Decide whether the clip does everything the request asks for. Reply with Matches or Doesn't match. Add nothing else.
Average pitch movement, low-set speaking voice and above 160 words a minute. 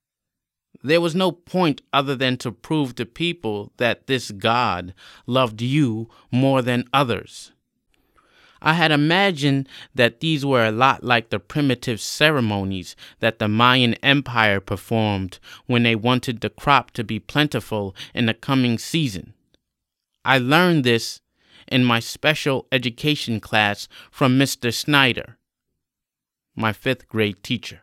Doesn't match